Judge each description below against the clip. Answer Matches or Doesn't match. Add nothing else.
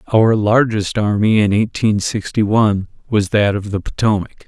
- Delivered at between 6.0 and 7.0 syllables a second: Doesn't match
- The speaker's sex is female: Doesn't match